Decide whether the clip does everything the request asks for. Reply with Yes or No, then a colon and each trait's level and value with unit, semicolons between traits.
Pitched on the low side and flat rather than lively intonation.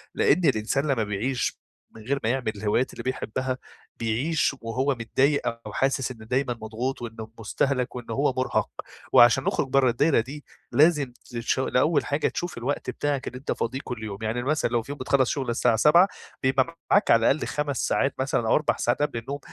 No: low, 130 Hz; average, 3.3 semitones